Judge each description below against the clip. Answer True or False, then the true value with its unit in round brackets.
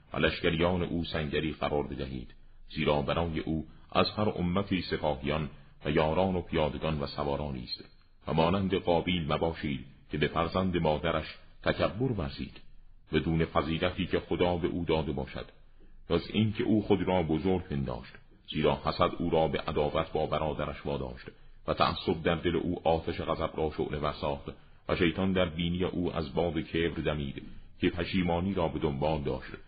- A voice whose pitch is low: True (80 Hz)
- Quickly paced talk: True (160 wpm)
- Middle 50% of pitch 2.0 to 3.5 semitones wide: True (3.1 semitones)